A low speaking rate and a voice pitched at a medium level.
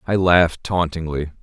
No: slow, 125 wpm; very low, 85 Hz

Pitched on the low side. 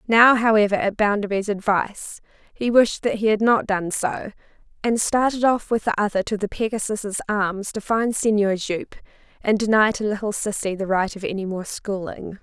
No: high, 210 Hz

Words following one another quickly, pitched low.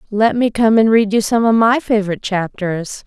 No: fast, 215 wpm; high, 215 Hz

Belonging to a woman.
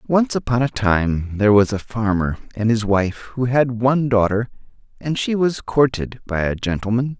No: male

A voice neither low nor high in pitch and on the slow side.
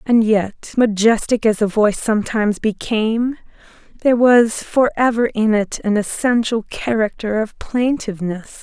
No: high, 220 Hz; slow, 130 wpm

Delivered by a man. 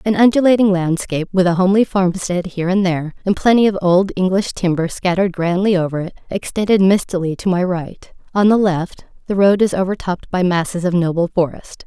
No: female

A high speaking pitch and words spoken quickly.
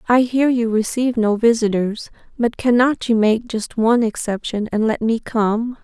No: high, 230 Hz; average, 175 wpm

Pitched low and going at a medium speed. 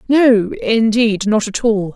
No: high, 220 Hz; average, 155 wpm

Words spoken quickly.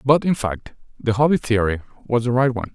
Yes: fast, 220 wpm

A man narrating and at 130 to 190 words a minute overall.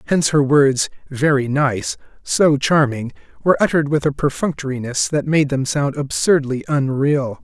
Yes: male; average, 145 wpm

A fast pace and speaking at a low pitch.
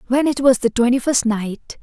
No: fast, 230 wpm; very high, 250 Hz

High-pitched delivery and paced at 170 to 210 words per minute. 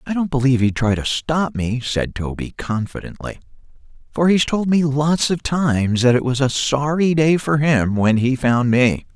No: low, 135 Hz; average, 195 wpm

